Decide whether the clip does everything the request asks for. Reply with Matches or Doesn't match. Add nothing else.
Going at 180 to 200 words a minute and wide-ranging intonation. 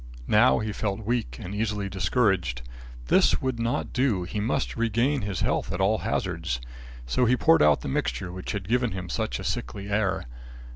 Doesn't match